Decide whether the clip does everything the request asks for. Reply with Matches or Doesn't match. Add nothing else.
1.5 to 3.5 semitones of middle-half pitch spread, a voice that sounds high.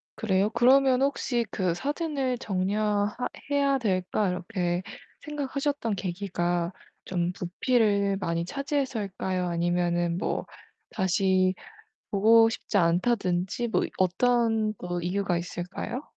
Doesn't match